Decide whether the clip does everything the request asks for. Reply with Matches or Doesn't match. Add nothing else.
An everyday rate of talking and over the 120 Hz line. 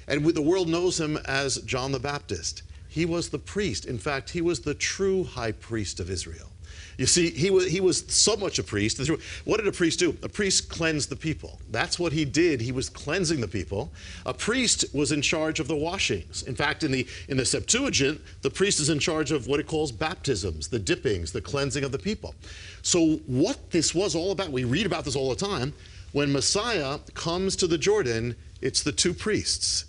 Doesn't match